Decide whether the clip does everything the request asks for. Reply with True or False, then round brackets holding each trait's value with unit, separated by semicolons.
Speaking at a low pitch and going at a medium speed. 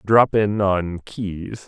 True (100 Hz; 145 wpm)